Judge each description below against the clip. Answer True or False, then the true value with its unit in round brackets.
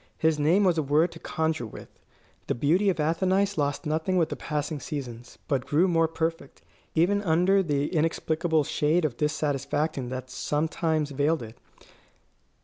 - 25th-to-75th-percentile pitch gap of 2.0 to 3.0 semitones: True (2.4 semitones)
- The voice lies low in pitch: False (155 Hz)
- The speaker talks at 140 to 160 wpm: True (155 wpm)